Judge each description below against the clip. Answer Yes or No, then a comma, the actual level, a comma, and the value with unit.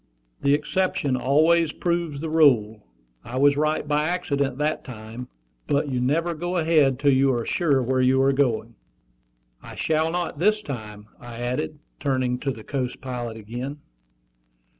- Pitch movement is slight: No, average, 3.7 semitones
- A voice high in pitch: No, medium, 140 Hz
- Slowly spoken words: No, average, 160 wpm